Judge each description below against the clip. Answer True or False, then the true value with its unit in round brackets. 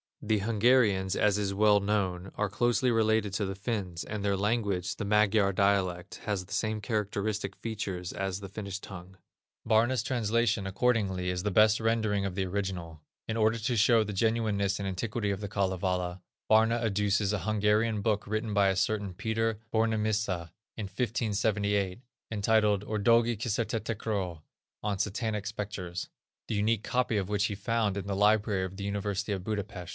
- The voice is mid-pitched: False (105 Hz)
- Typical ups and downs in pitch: False (2.2 semitones)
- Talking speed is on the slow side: False (165 wpm)